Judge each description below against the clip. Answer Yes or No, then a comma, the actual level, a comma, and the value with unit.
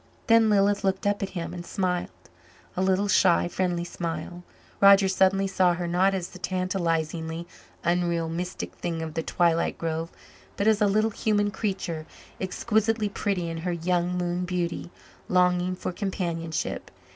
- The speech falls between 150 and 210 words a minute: Yes, average, 155 wpm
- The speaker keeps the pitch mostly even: Yes, narrow, 2.2 semitones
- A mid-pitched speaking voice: Yes, medium, 180 Hz